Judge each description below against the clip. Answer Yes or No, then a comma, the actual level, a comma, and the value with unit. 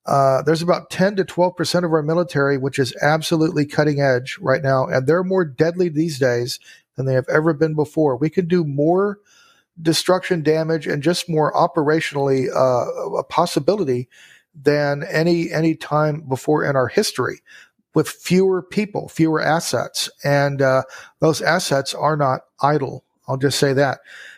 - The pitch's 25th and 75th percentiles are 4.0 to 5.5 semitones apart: No, average, 3.5 semitones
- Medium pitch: Yes, medium, 155 Hz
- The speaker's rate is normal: Yes, average, 160 wpm